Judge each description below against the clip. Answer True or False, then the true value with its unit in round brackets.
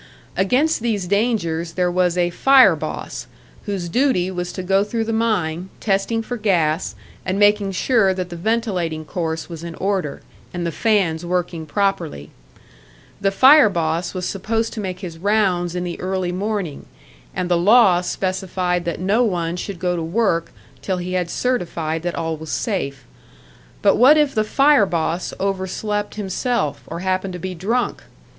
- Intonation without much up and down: False (3.5 semitones)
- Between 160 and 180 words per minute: True (165 wpm)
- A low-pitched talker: False (185 Hz)